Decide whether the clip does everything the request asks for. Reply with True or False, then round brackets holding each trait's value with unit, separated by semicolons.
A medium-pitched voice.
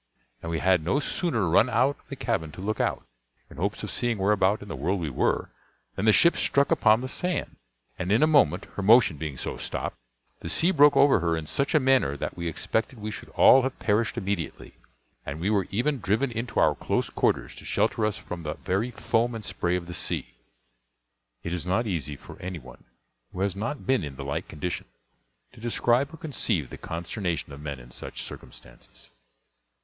False (100 Hz)